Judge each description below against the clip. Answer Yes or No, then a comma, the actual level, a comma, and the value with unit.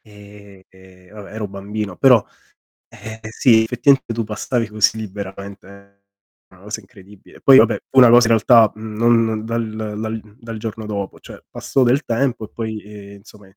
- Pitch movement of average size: No, narrow, 2.1 semitones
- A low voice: Yes, low, 110 Hz